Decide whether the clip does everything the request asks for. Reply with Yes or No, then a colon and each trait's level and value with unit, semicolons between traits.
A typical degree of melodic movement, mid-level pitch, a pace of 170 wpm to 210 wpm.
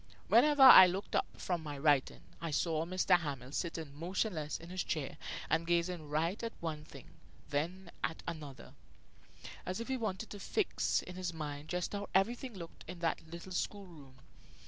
Yes: average, 3.4 semitones; medium, 170 Hz; average, 175 wpm